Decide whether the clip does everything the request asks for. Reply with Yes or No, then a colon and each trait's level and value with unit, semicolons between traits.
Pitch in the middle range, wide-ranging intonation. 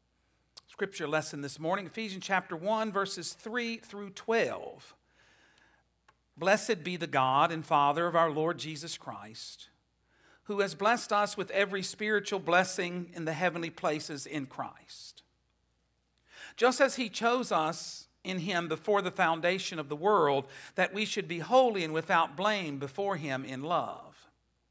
No: medium, 180 Hz; average, 4.5 semitones